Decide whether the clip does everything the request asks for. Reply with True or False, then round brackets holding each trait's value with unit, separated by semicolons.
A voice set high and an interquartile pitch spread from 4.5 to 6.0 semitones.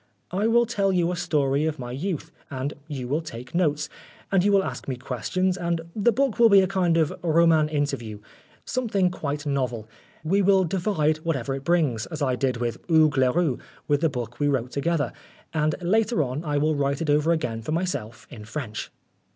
False (155 Hz; 5.0 semitones)